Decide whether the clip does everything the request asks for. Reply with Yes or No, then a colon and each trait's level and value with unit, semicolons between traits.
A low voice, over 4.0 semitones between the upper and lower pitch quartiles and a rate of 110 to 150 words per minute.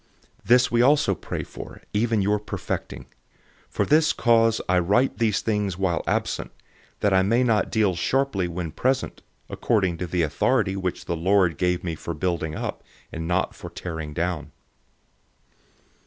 No: very low, 95 Hz; average, 4.7 semitones; average, 165 wpm